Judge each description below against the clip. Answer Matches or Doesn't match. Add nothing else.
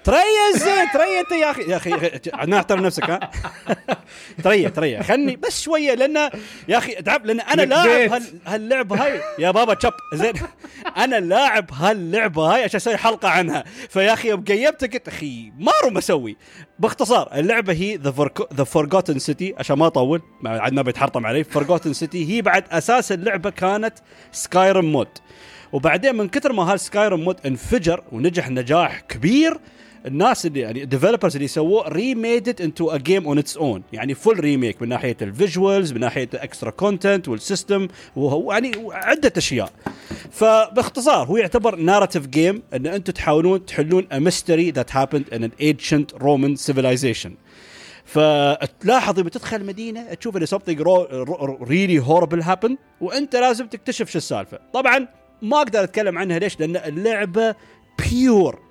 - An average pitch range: Doesn't match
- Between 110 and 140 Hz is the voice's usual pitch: Doesn't match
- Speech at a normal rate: Doesn't match